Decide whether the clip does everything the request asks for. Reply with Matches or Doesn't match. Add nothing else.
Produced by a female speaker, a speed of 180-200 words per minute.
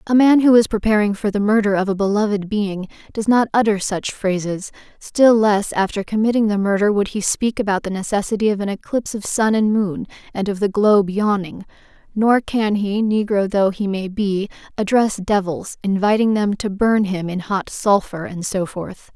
Matches